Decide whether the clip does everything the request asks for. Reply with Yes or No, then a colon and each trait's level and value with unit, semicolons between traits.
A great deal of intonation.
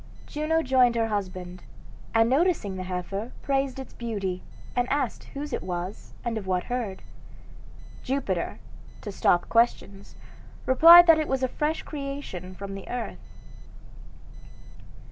Yes: wide, 6.3 semitones